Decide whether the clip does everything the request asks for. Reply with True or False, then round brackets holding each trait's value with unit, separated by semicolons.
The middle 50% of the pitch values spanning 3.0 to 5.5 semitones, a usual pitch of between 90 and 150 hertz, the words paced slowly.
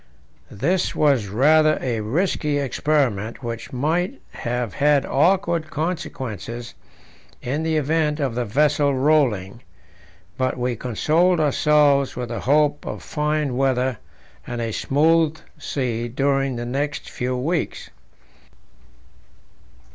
True (3.9 semitones; 140 Hz; 115 wpm)